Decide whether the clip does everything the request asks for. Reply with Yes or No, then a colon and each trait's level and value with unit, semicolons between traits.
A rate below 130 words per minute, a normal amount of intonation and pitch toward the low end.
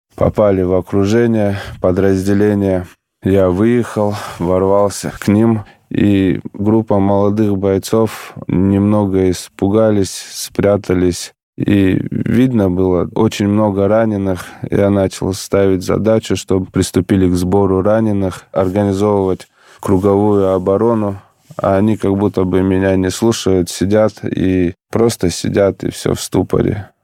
No: slow, 110 wpm; narrow, 1.9 semitones; low, 100 Hz